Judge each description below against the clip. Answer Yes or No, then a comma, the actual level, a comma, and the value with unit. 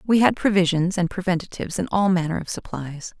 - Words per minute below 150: No, average, 190 wpm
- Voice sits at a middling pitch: Yes, medium, 180 Hz